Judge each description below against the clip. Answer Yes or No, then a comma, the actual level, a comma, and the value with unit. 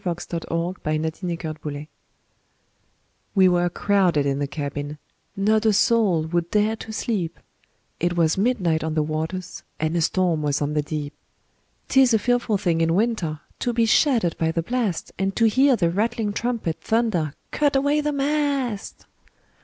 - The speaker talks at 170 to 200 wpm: Yes, average, 175 wpm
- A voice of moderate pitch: Yes, medium, 180 Hz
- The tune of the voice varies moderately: No, wide, 6.2 semitones